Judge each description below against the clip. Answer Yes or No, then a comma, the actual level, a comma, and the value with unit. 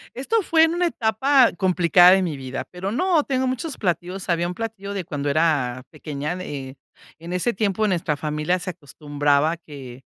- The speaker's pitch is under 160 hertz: No, medium, 180 Hz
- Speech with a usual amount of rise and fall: No, wide, 6.7 semitones